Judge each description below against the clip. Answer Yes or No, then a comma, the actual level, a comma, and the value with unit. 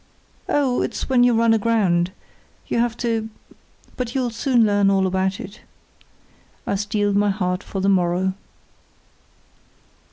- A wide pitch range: No, average, 3.4 semitones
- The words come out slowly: Yes, slow, 130 wpm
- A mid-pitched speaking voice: No, high, 205 Hz